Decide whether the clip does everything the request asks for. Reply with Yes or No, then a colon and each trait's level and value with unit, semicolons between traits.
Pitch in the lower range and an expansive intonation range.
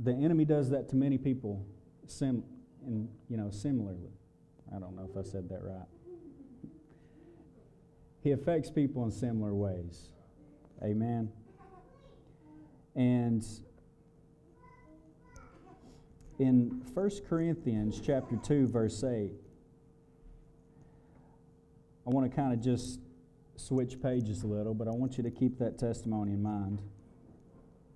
Yes: low, 125 Hz; wide, 5.8 semitones